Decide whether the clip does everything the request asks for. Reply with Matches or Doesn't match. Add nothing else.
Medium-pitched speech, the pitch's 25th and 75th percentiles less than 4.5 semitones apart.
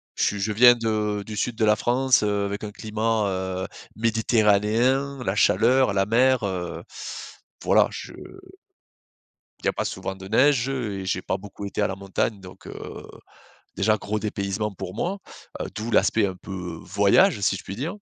Doesn't match